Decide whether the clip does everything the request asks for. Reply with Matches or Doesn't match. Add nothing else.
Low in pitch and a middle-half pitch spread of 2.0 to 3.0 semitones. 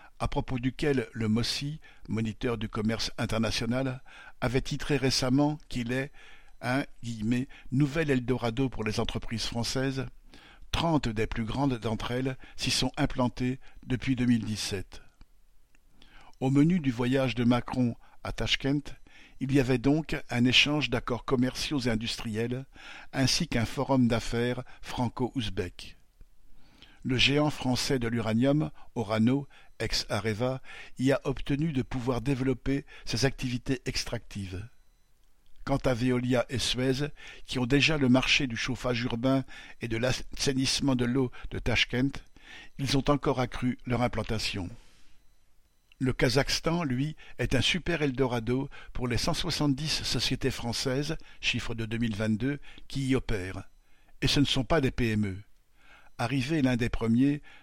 Matches